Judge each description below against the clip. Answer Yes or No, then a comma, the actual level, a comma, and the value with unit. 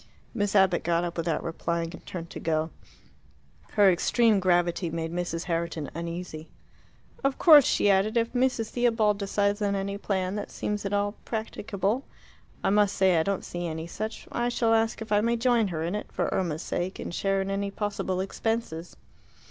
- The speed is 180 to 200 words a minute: Yes, average, 185 wpm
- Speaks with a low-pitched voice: No, high, 195 Hz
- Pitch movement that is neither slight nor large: Yes, average, 4.0 semitones